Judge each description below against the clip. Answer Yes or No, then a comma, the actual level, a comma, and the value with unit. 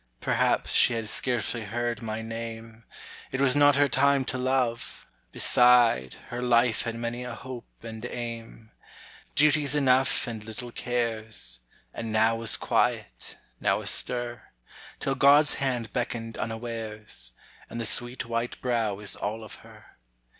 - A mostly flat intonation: Yes, narrow, 1.9 semitones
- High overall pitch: No, low, 115 Hz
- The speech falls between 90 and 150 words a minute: Yes, average, 140 wpm